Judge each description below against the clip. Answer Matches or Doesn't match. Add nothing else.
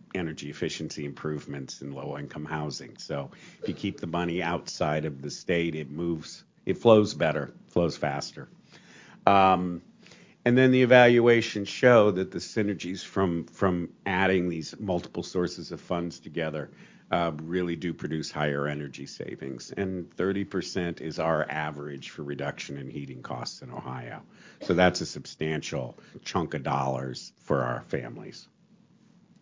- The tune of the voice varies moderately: Matches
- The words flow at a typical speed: Matches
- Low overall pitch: Matches